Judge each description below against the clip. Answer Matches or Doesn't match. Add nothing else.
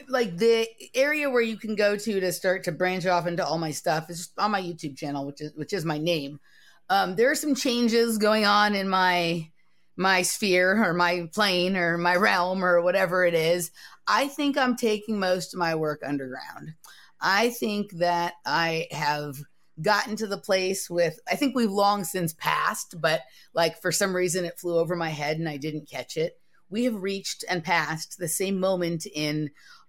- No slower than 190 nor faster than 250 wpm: Matches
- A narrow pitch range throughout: Doesn't match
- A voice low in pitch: Doesn't match